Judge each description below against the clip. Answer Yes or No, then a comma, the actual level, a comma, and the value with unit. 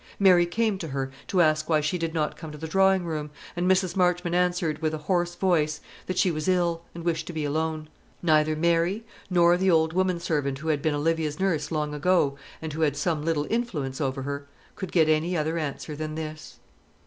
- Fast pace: Yes, fast, 215 wpm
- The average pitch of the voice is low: No, medium, 160 Hz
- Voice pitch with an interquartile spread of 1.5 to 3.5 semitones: Yes, average, 2.7 semitones